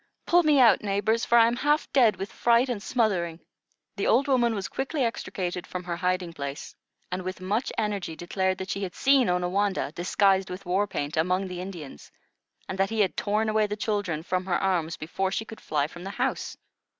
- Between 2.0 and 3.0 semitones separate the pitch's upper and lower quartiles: No, average, 3.8 semitones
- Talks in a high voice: Yes, high, 195 Hz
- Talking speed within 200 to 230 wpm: Yes, fast, 205 wpm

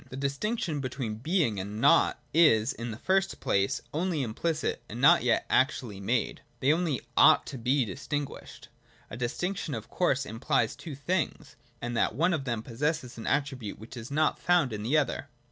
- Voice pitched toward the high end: No, low, 135 Hz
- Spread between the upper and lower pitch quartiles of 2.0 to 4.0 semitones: No, average, 5.1 semitones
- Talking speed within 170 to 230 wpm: Yes, average, 180 wpm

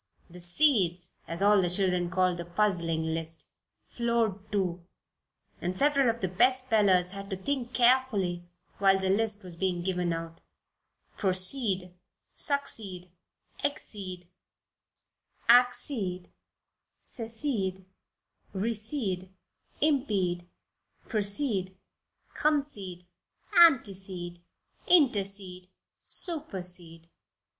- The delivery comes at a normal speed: No, slow, 90 wpm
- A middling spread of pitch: Yes, average, 4.6 semitones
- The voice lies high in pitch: Yes, high, 195 Hz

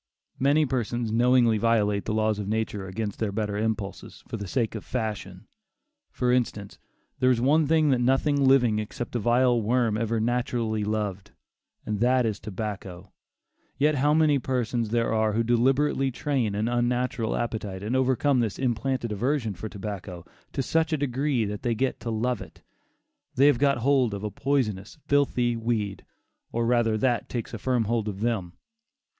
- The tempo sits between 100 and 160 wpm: No, average, 175 wpm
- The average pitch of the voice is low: Yes, low, 115 Hz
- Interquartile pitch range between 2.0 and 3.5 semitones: Yes, average, 3.2 semitones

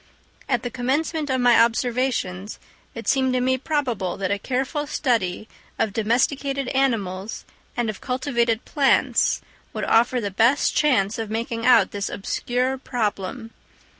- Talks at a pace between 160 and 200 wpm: No, average, 140 wpm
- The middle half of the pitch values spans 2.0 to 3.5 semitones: Yes, average, 3.2 semitones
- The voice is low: No, high, 245 Hz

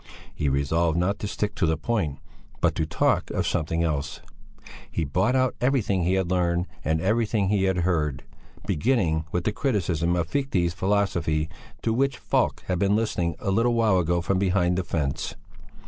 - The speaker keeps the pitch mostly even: No, average, 4.2 semitones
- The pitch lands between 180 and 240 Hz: No, very low, 90 Hz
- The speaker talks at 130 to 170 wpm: No, average, 180 wpm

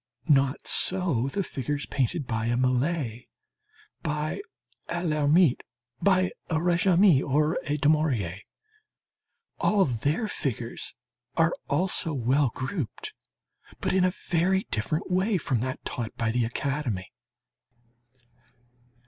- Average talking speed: No, slow, 115 wpm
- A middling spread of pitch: No, wide, 5.7 semitones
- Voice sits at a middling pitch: Yes, medium, 150 Hz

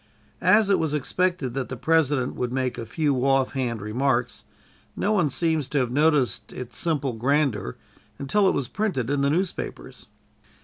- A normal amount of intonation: Yes, average, 4.2 semitones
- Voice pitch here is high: No, low, 135 Hz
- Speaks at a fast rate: No, average, 165 wpm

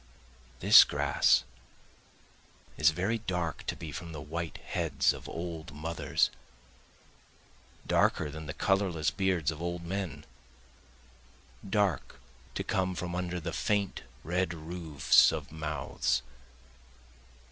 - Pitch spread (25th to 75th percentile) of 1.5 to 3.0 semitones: Yes, narrow, 2.6 semitones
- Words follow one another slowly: Yes, slow, 115 wpm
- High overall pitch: No, very low, 85 Hz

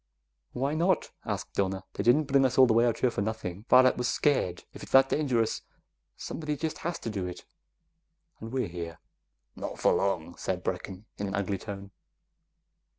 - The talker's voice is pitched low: Yes, low, 115 Hz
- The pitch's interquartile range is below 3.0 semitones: No, wide, 5.6 semitones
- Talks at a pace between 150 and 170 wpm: No, average, 185 wpm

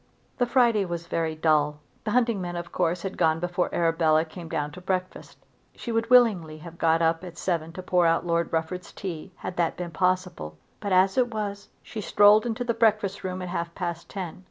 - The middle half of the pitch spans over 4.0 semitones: No, average, 3.4 semitones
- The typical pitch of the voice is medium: Yes, medium, 180 Hz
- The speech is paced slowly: No, fast, 205 wpm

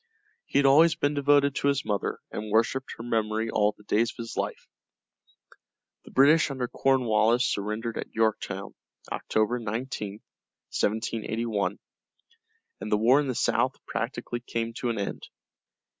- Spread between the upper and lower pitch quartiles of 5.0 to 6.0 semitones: No, average, 3.4 semitones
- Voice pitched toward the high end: No, low, 115 Hz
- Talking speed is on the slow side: No, average, 145 wpm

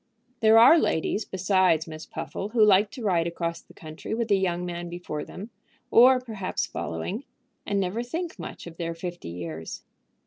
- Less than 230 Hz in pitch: Yes, medium, 185 Hz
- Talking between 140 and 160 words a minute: No, average, 175 wpm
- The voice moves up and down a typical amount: Yes, average, 4.6 semitones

